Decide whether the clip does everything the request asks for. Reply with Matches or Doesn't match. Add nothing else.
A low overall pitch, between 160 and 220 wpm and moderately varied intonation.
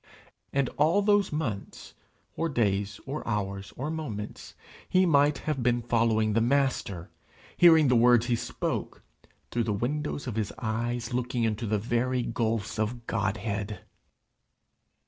Doesn't match